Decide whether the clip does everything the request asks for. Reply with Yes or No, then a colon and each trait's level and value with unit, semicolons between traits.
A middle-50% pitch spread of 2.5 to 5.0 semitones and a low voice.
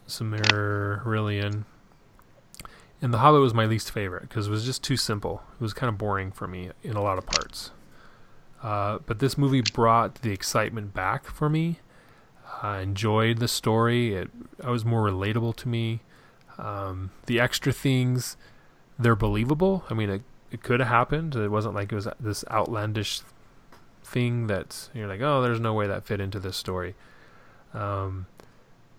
Yes: average, 3.0 semitones; low, 110 Hz